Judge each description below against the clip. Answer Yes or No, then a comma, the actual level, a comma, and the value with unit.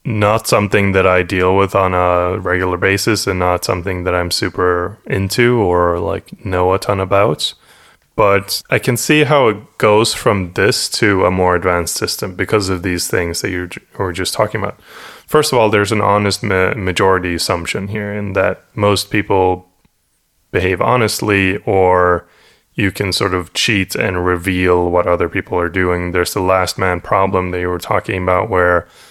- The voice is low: Yes, very low, 95 Hz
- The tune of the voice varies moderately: No, narrow, 2.3 semitones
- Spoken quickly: No, average, 180 wpm